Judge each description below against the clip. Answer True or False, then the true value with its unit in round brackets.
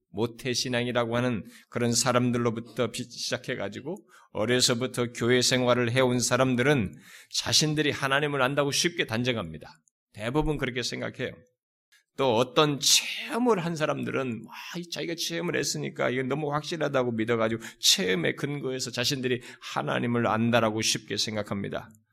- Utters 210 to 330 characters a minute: False (350 characters per minute)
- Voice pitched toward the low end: True (125 Hz)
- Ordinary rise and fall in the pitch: True (3.2 semitones)